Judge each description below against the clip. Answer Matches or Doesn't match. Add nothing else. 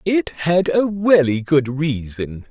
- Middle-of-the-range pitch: Matches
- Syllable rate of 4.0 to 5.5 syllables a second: Doesn't match